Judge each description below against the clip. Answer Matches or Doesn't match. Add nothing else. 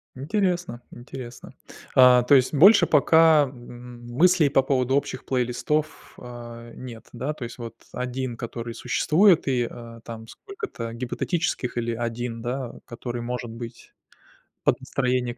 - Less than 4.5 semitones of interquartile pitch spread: Matches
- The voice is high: Doesn't match